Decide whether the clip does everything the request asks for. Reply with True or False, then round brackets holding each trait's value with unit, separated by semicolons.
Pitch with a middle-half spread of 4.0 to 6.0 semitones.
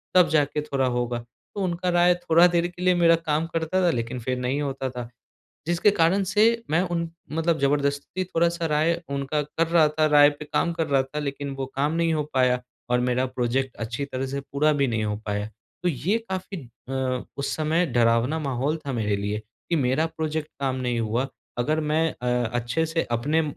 True (4.5 semitones)